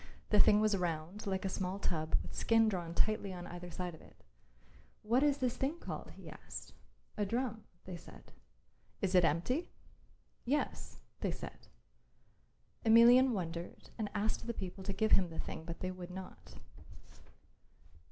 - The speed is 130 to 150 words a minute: No, average, 160 wpm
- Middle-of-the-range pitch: No, high, 195 Hz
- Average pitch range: Yes, average, 4.3 semitones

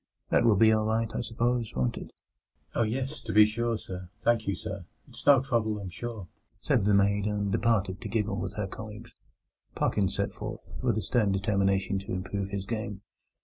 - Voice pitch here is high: No, low, 105 Hz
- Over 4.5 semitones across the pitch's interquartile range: No, narrow, 2.6 semitones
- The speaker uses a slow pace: No, average, 195 wpm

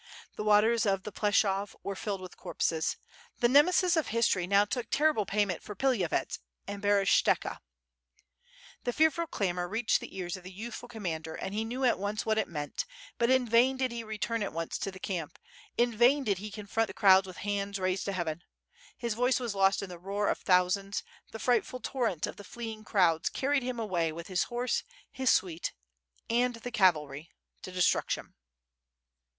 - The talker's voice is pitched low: No, high, 205 Hz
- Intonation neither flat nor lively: Yes, average, 4.2 semitones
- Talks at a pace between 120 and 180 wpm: No, average, 190 wpm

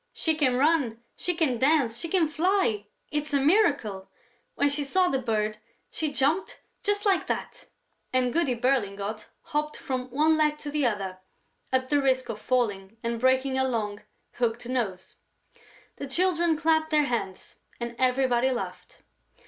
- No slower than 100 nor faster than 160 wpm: Yes, average, 155 wpm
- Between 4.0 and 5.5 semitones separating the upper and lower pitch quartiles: Yes, average, 4.7 semitones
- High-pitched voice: Yes, very high, 265 Hz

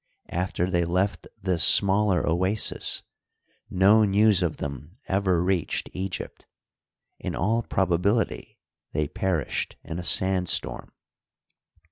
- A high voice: No, very low, 95 Hz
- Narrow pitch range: Yes, narrow, 2.3 semitones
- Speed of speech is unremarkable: No, slow, 110 wpm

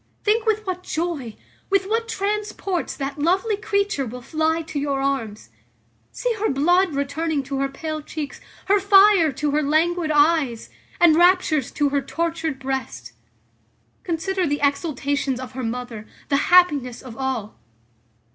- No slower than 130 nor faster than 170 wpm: Yes, average, 145 wpm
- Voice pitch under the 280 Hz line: No, very high, 310 Hz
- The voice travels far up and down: No, average, 5.0 semitones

